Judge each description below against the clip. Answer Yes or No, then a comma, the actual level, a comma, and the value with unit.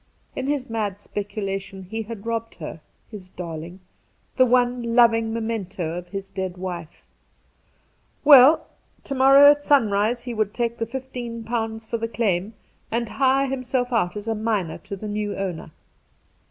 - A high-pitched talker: Yes, high, 225 Hz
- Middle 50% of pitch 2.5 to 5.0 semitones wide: Yes, average, 3.8 semitones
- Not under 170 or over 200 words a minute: No, average, 155 wpm